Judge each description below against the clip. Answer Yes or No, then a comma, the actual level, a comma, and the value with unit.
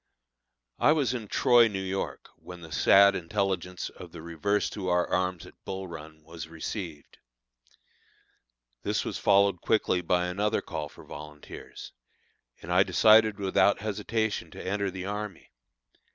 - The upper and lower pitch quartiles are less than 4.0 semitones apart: Yes, average, 3.3 semitones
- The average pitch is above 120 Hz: No, very low, 95 Hz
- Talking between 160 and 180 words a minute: No, average, 145 wpm